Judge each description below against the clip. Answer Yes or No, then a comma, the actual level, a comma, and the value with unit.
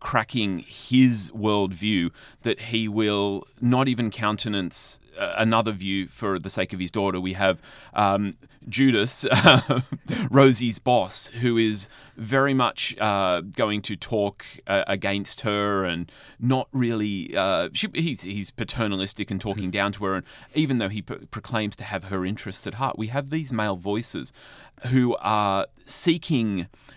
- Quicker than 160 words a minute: No, average, 150 wpm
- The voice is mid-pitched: No, low, 105 Hz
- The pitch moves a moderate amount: Yes, average, 3.9 semitones